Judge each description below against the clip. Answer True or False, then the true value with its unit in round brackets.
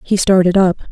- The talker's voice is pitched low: False (185 Hz)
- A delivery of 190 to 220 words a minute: True (195 wpm)